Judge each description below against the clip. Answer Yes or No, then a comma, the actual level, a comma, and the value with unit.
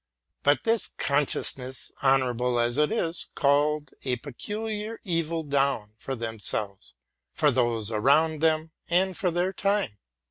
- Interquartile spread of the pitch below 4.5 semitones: No, average, 5.1 semitones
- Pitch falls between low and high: Yes, medium, 145 Hz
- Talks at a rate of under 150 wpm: Yes, slow, 135 wpm